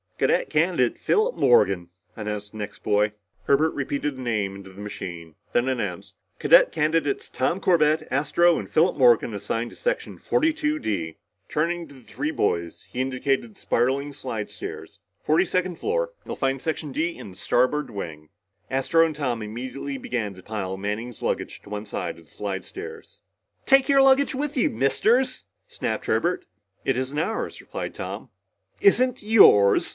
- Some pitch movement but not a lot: No, wide, 8.8 semitones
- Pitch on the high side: No, low, 135 Hz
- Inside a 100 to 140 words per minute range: No, average, 160 wpm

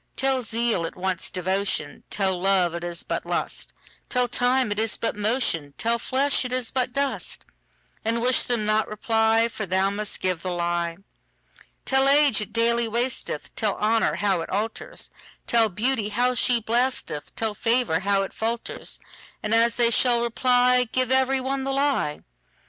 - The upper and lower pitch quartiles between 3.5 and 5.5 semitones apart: Yes, average, 4.1 semitones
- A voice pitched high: Yes, high, 225 Hz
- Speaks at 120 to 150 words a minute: Yes, average, 140 wpm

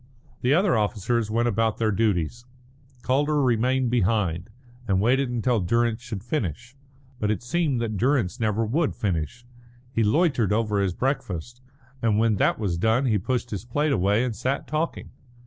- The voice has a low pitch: Yes, low, 115 Hz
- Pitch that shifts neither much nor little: Yes, average, 3.5 semitones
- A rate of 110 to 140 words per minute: No, average, 165 wpm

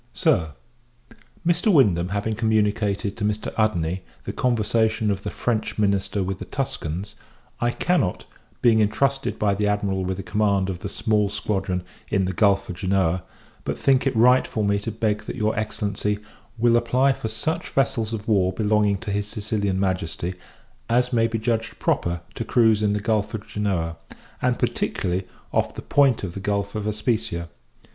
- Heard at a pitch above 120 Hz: No, low, 105 Hz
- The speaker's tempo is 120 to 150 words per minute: No, average, 175 wpm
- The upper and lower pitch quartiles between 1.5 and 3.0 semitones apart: Yes, narrow, 2.6 semitones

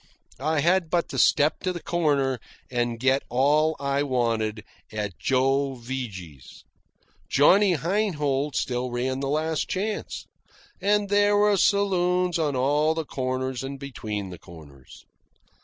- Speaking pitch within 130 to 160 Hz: Yes, medium, 140 Hz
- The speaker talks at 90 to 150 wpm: Yes, slow, 135 wpm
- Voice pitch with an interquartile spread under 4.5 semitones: No, wide, 5.4 semitones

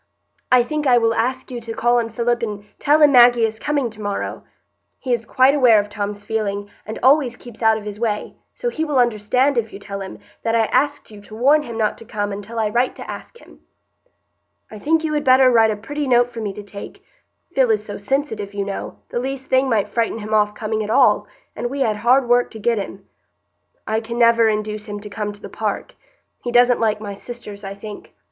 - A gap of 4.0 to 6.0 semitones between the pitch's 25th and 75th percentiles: No, average, 3.1 semitones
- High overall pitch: Yes, high, 230 Hz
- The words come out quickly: Yes, fast, 235 wpm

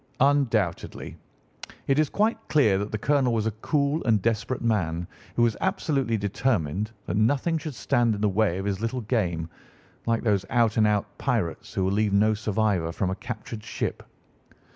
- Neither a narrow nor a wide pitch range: Yes, average, 3.8 semitones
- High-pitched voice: No, low, 110 Hz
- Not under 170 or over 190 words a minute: Yes, average, 180 wpm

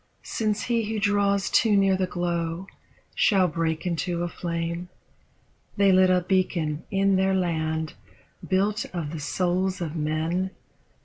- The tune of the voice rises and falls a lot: No, average, 2.7 semitones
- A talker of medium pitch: Yes, medium, 180 Hz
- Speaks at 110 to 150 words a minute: Yes, average, 140 wpm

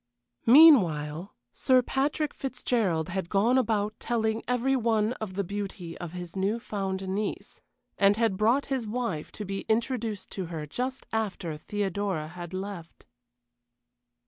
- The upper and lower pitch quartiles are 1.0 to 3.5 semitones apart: No, average, 4.2 semitones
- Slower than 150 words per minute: Yes, average, 140 wpm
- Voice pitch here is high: Yes, high, 205 Hz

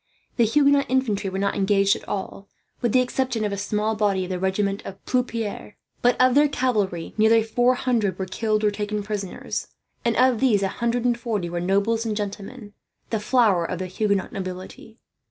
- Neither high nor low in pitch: No, high, 210 Hz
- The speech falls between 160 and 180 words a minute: No, average, 190 wpm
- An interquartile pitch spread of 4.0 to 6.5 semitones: No, average, 3.4 semitones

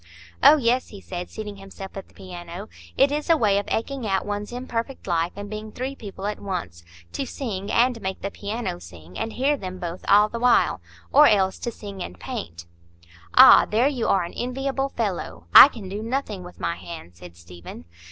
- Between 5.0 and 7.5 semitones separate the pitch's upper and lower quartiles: Yes, average, 5.3 semitones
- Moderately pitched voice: No, high, 205 Hz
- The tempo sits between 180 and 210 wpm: Yes, average, 195 wpm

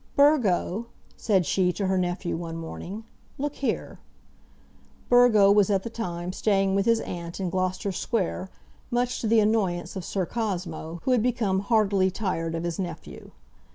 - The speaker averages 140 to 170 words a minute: Yes, average, 160 wpm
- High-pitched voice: Yes, high, 195 Hz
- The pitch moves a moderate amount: Yes, average, 4.1 semitones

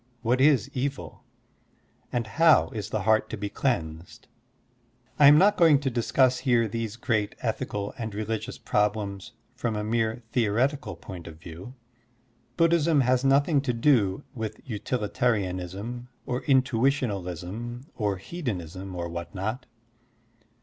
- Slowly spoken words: Yes, slow, 130 wpm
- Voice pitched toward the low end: Yes, low, 115 Hz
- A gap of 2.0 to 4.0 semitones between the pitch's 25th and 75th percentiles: No, average, 4.5 semitones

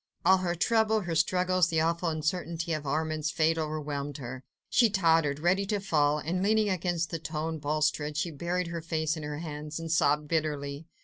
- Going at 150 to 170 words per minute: No, average, 185 wpm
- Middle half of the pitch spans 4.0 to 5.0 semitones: No, narrow, 2.6 semitones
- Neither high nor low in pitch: Yes, medium, 160 Hz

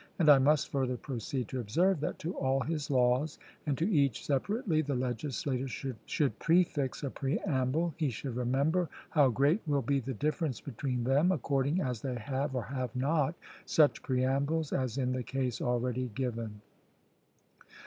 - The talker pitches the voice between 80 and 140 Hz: Yes, low, 135 Hz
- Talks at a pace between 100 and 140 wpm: No, average, 160 wpm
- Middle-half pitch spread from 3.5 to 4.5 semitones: No, average, 3.0 semitones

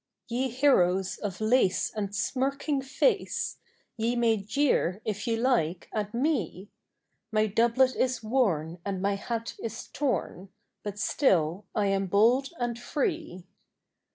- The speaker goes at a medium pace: No, slow, 130 wpm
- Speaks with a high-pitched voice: Yes, high, 225 Hz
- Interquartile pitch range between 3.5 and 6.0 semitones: Yes, average, 4.6 semitones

